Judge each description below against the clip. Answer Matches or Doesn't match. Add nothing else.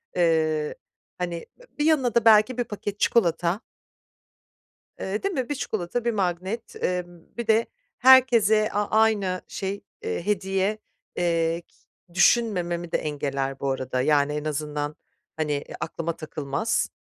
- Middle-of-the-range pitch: Matches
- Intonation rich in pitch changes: Matches